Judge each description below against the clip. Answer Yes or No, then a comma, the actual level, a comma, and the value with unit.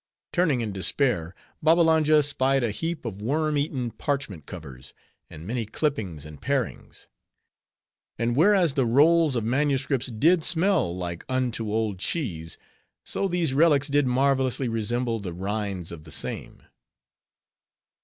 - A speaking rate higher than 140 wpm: No, slow, 135 wpm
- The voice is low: Yes, low, 125 Hz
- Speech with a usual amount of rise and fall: No, wide, 6.3 semitones